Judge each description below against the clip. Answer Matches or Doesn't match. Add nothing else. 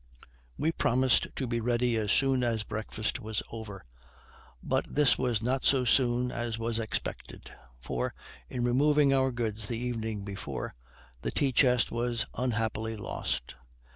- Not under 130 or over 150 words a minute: Matches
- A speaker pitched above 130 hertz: Doesn't match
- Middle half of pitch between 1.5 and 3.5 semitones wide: Matches